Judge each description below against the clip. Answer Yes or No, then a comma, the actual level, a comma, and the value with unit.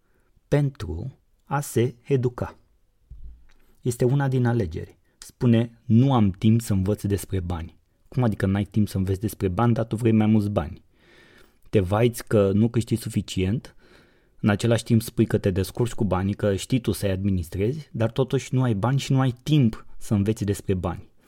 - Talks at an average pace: No, fast, 180 wpm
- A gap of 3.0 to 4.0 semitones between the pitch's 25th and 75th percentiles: Yes, average, 3.7 semitones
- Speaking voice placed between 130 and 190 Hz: No, low, 110 Hz